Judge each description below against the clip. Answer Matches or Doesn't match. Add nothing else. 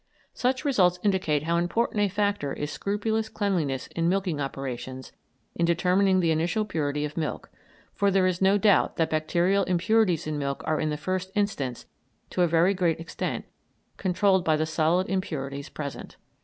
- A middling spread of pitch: Matches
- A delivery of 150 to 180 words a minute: Matches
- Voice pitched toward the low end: Doesn't match